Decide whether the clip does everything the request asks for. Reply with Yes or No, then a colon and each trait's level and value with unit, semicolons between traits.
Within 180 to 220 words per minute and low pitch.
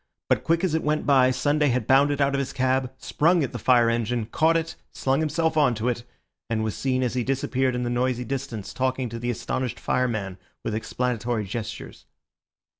Yes: average, 200 wpm; low, 130 Hz